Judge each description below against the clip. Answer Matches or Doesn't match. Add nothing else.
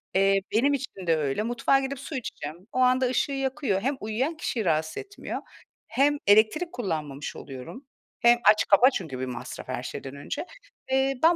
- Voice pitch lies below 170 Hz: Doesn't match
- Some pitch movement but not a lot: Doesn't match